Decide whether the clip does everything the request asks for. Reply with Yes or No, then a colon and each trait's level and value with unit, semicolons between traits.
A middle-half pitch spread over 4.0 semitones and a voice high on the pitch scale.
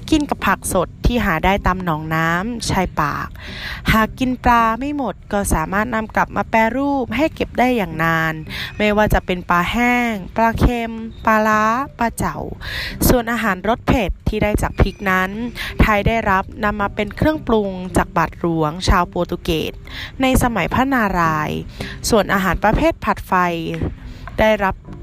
Yes: average, 4.5 semitones; high, 210 Hz